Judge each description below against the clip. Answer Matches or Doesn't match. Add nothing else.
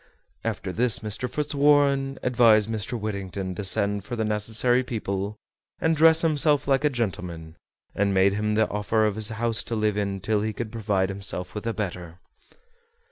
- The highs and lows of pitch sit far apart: Doesn't match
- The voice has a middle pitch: Doesn't match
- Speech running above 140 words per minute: Matches